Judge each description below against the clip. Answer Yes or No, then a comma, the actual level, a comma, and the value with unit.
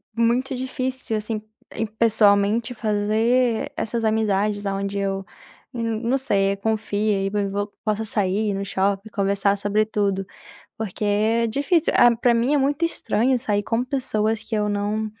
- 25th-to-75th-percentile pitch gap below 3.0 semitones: Yes, narrow, 2.4 semitones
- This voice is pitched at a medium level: No, high, 215 Hz